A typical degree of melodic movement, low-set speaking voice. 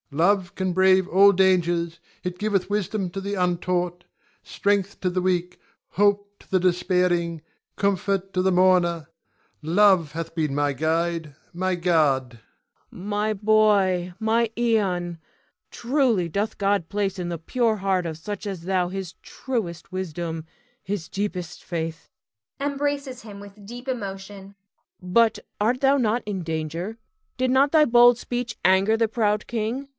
No: average, 3.3 semitones; high, 190 Hz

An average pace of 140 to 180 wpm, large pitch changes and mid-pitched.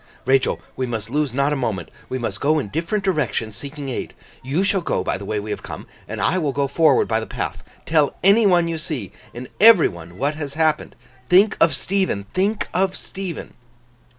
No: fast, 205 wpm; wide, 6.8 semitones; medium, 145 Hz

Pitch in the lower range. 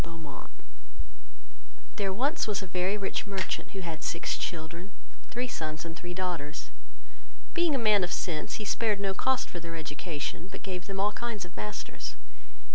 No: high, 190 Hz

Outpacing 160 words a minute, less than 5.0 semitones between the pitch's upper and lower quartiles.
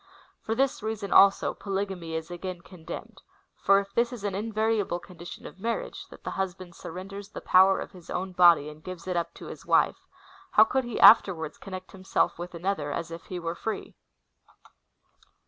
Yes: average, 185 wpm; average, 2.8 semitones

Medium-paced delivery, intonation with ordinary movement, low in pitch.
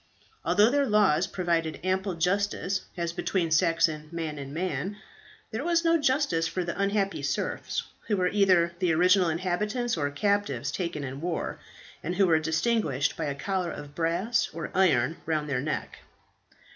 No: average, 160 wpm; average, 4.0 semitones; medium, 180 Hz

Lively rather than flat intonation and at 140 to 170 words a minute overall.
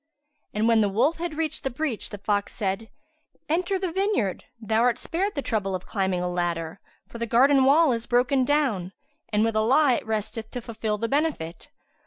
No: wide, 5.8 semitones; average, 195 wpm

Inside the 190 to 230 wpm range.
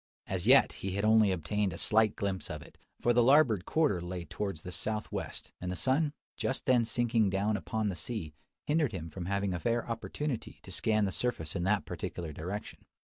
Yes: fast, 205 wpm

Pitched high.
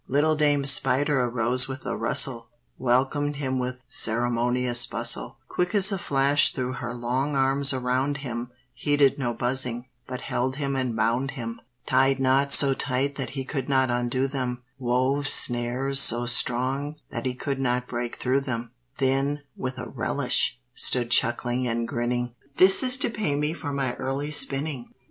No: low, 130 Hz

